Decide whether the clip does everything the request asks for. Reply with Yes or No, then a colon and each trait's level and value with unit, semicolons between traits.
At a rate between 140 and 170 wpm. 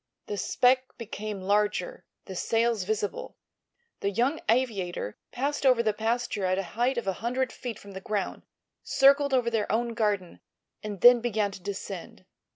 Yes: average, 165 wpm